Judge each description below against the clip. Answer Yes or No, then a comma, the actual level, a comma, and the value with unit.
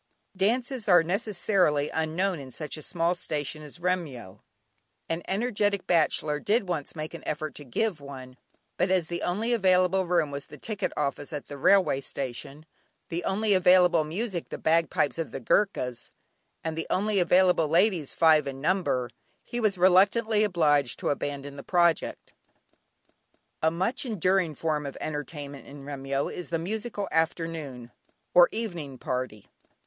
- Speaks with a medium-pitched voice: Yes, medium, 165 Hz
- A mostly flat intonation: No, average, 4.6 semitones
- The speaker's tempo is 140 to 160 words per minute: Yes, average, 155 wpm